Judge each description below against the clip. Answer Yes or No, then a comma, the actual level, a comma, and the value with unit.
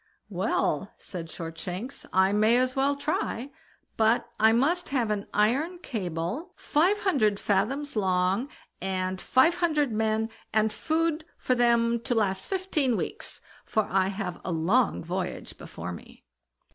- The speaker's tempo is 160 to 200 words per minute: No, average, 140 wpm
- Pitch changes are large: Yes, wide, 6.6 semitones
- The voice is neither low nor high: No, high, 225 Hz